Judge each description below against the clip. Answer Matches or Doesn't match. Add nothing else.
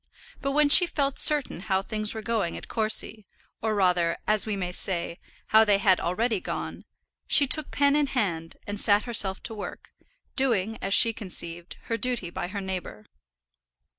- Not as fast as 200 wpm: Matches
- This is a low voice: Doesn't match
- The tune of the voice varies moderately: Matches